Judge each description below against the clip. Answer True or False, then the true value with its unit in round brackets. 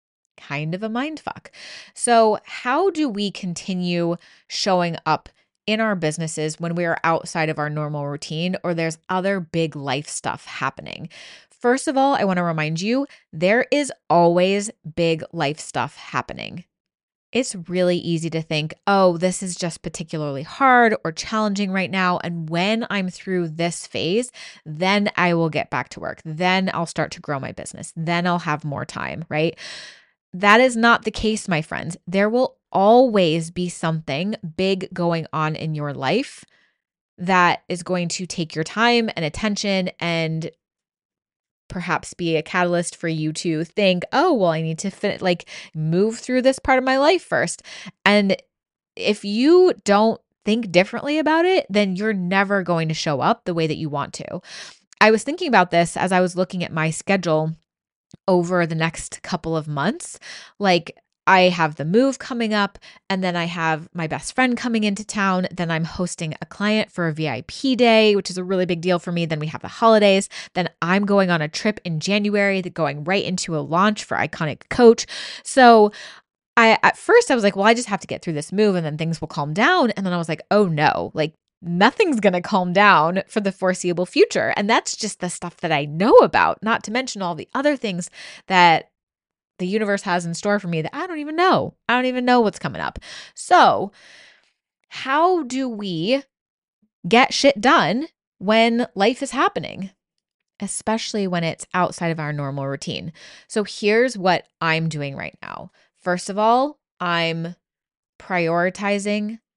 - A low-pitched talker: False (185 Hz)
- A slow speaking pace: False (185 wpm)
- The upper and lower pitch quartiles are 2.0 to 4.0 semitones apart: False (4.6 semitones)